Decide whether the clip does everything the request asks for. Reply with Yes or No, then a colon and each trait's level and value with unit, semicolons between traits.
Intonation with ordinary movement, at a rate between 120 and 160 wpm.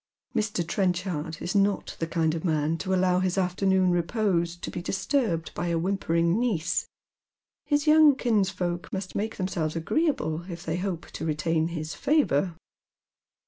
Yes: average, 3.2 semitones; average, 150 wpm